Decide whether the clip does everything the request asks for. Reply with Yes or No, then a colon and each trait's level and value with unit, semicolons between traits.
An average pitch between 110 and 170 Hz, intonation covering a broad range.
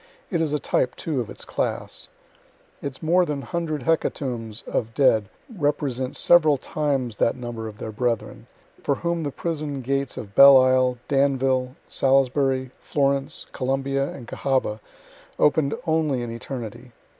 No: low, 135 Hz; average, 2.8 semitones